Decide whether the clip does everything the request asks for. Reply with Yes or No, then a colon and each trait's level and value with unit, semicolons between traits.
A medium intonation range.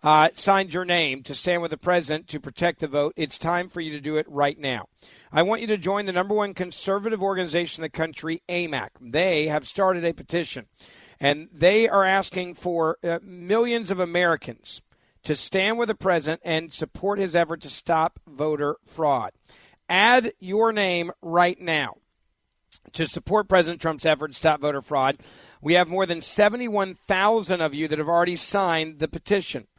Yes: average, 3.6 semitones